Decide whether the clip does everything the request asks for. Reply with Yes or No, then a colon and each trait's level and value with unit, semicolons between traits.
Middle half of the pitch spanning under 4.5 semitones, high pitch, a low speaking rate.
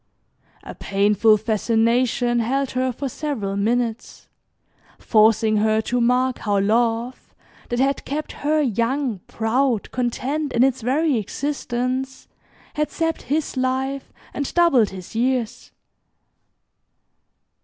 Yes: average, 3.3 semitones; high, 245 Hz; slow, 110 wpm